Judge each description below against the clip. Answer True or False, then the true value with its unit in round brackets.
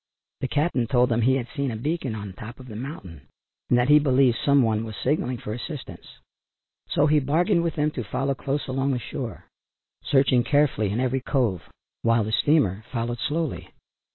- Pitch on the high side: False (130 Hz)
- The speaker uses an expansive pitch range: False (3.9 semitones)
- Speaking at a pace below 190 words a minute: False (195 wpm)